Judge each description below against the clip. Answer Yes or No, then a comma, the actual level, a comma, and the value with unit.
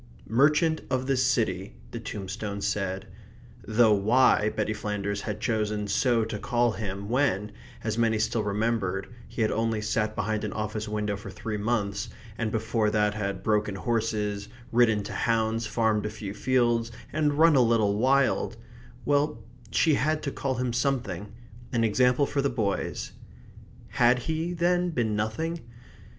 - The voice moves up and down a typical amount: Yes, average, 3.2 semitones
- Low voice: Yes, low, 110 Hz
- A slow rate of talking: No, average, 155 wpm